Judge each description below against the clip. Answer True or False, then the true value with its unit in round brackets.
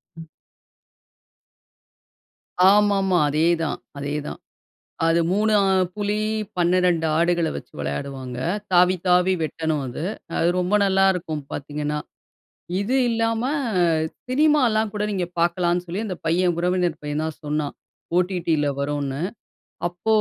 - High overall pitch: False (175 Hz)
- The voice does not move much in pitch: False (4.0 semitones)